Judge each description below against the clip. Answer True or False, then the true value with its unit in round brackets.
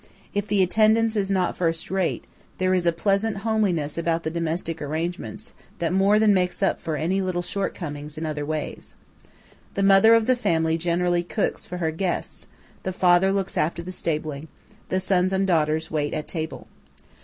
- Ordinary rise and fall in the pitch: True (3.2 semitones)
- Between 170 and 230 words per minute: True (180 wpm)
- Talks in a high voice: False (180 Hz)